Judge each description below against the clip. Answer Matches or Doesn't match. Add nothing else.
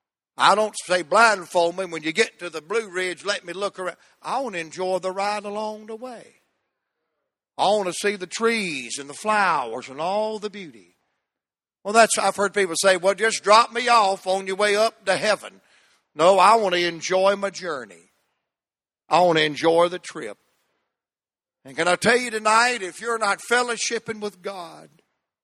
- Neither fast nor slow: Matches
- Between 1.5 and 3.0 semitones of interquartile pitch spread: Doesn't match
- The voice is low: Doesn't match